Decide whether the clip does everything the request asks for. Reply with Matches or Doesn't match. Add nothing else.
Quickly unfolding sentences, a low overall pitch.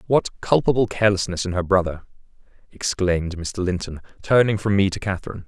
Doesn't match